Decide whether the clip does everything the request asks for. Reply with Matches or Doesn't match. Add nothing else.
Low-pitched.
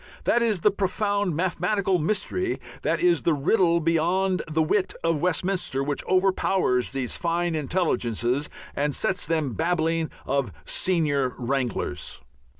Doesn't match